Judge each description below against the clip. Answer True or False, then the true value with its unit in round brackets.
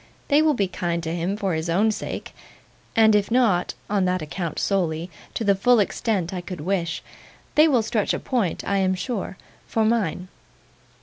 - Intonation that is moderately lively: True (4.0 semitones)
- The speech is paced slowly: False (185 wpm)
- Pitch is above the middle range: True (195 Hz)